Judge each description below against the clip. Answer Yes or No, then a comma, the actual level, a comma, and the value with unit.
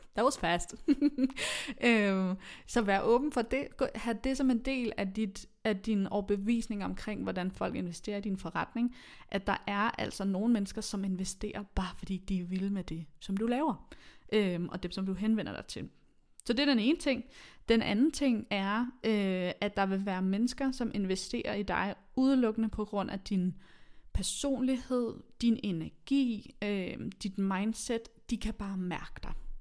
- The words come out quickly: No, average, 180 wpm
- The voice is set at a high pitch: Yes, high, 210 Hz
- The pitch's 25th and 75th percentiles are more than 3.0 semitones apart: Yes, average, 3.6 semitones